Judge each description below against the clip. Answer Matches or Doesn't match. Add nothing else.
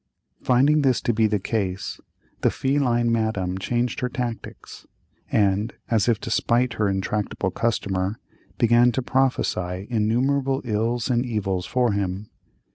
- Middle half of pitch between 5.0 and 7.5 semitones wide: Doesn't match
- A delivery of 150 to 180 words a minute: Doesn't match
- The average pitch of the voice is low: Matches